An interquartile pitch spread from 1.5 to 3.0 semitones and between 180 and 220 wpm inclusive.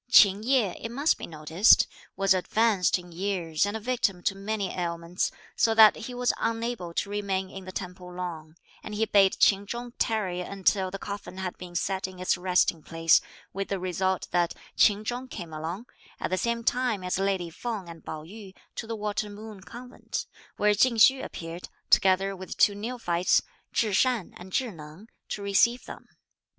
No: average, 3.5 semitones; average, 185 wpm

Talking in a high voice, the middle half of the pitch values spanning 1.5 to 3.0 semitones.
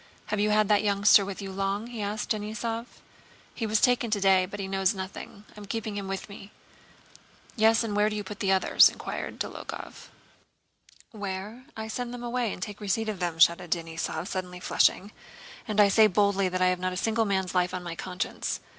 Yes: high, 205 Hz; narrow, 2.4 semitones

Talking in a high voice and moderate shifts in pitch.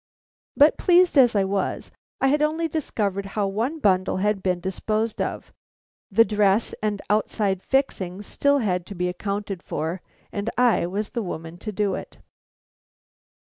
Yes: high, 205 Hz; average, 3.9 semitones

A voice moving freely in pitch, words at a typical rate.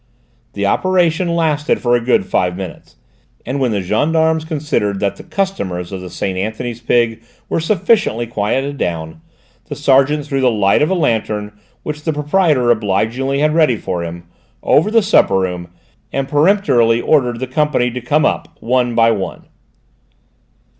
Yes: wide, 6.6 semitones; average, 160 wpm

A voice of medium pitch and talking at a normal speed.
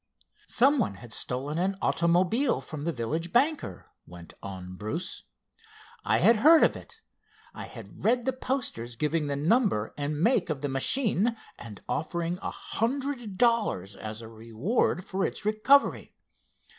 Yes: medium, 170 Hz; average, 150 wpm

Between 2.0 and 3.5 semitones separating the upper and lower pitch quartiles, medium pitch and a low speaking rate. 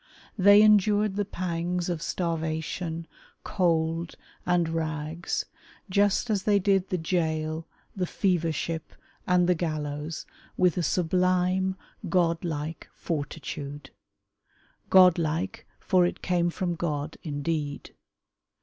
Yes: narrow, 2.4 semitones; medium, 170 Hz; slow, 105 wpm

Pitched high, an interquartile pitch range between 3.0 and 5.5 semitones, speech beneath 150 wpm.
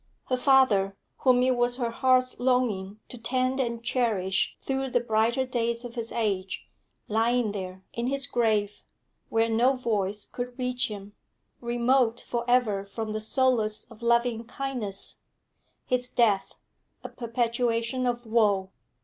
No: high, 235 Hz; narrow, 2.6 semitones; average, 140 wpm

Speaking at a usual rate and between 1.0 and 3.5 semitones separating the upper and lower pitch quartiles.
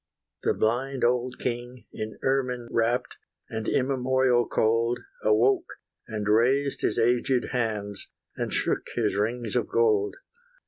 No: slow, 125 wpm; narrow, 2.6 semitones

